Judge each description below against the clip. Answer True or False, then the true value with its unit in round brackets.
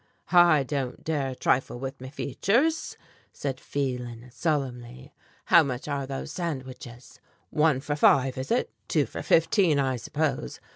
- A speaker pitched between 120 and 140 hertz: True (135 Hz)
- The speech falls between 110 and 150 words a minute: True (140 wpm)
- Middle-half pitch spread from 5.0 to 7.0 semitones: False (3.2 semitones)